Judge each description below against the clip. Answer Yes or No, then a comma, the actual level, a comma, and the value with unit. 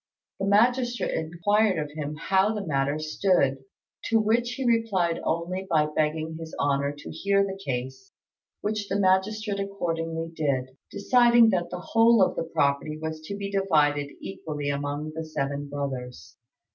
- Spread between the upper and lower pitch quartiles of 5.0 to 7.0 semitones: Yes, wide, 5.6 semitones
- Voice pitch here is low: No, medium, 165 Hz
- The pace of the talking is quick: No, average, 155 wpm